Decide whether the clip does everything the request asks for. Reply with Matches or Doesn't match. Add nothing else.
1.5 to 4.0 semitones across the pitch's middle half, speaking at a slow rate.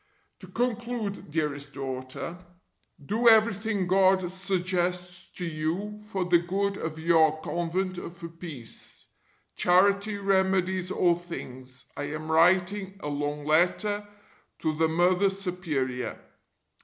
Matches